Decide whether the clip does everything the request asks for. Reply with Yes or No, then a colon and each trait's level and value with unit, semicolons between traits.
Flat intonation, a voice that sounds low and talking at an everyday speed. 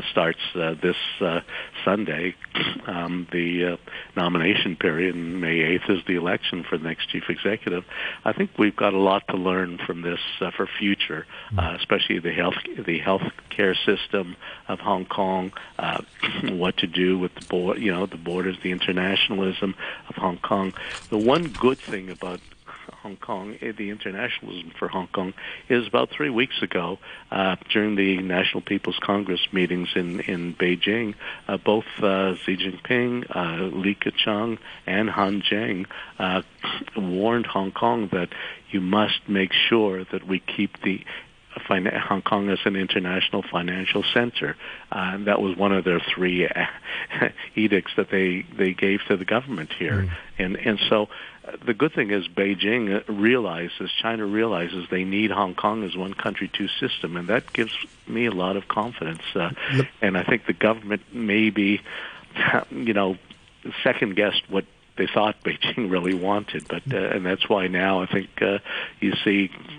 Yes: narrow, 2.3 semitones; very low, 95 Hz; average, 170 wpm